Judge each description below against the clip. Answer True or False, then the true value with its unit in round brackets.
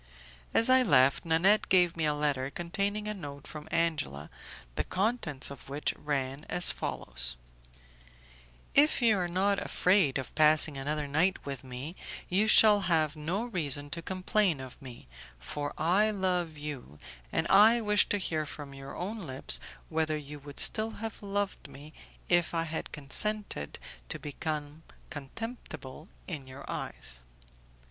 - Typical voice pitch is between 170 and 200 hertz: False (160 Hz)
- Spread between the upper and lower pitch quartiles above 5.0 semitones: True (5.5 semitones)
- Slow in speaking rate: False (150 wpm)